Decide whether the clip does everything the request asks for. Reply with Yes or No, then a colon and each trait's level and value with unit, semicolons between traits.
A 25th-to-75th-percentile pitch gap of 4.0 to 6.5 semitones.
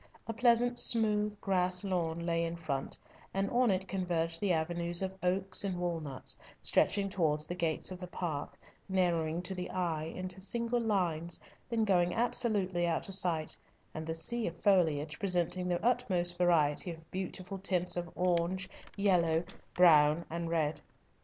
No: average, 2.7 semitones